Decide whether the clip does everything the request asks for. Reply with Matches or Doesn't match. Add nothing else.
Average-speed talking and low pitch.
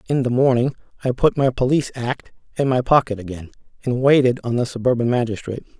Matches